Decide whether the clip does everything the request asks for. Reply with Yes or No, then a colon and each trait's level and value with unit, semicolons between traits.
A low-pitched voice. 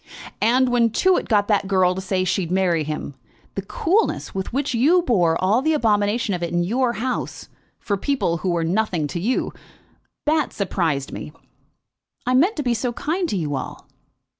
No: high, 205 Hz